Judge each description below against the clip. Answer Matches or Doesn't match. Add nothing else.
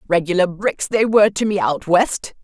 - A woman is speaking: Matches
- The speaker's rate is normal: Matches